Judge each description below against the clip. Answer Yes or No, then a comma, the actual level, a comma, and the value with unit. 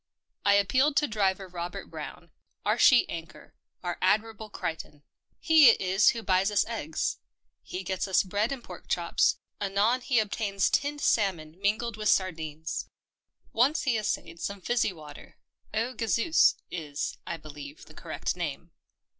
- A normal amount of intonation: Yes, average, 4.5 semitones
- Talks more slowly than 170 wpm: Yes, average, 160 wpm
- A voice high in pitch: Yes, high, 200 Hz